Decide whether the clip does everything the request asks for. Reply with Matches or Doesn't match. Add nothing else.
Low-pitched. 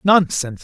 Doesn't match